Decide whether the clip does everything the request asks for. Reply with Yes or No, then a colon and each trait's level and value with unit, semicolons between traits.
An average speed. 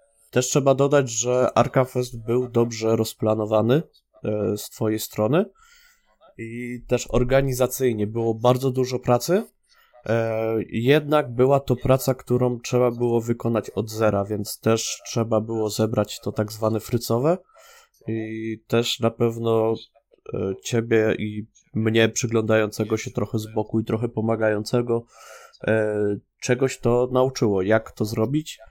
Yes: average, 130 wpm